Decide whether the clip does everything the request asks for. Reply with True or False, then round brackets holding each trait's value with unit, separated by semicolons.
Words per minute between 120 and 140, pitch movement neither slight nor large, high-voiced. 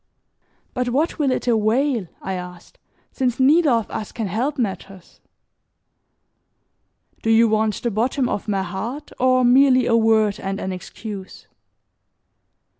True (135 wpm; 4.2 semitones; 225 Hz)